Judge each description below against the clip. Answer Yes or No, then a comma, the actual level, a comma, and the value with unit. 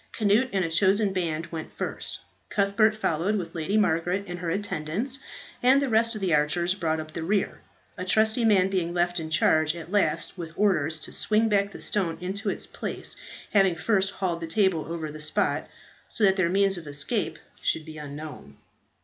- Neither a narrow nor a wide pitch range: Yes, average, 4.0 semitones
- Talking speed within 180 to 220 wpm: Yes, average, 190 wpm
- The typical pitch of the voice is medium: Yes, medium, 180 Hz